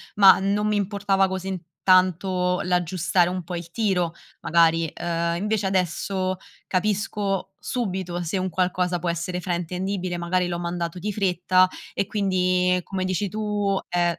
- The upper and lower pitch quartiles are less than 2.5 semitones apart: Yes, narrow, 1.8 semitones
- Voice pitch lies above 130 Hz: Yes, medium, 185 Hz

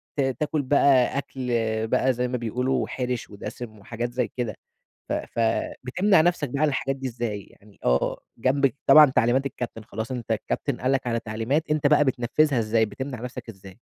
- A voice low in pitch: Yes, low, 125 Hz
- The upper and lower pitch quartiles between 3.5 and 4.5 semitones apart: No, average, 3.1 semitones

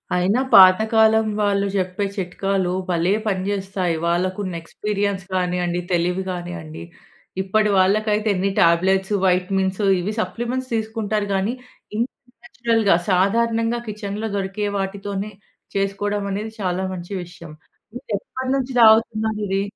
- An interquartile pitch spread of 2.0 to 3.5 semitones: Yes, average, 2.8 semitones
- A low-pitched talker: No, high, 195 Hz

